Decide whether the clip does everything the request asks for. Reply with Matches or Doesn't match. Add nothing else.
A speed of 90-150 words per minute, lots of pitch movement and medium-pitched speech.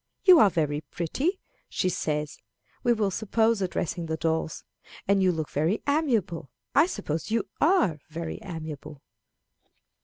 Matches